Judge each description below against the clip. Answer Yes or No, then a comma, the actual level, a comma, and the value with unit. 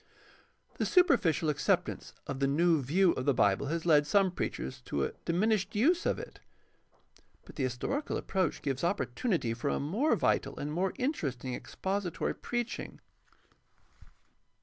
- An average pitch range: No, wide, 6.4 semitones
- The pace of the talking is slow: No, average, 150 wpm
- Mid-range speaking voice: Yes, medium, 170 Hz